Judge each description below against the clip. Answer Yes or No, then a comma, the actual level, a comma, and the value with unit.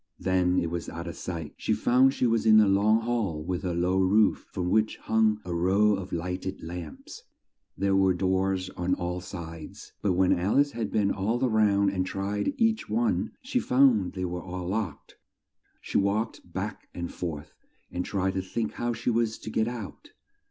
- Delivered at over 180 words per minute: Yes, average, 195 wpm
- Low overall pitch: Yes, very low, 95 Hz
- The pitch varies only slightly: No, average, 3.4 semitones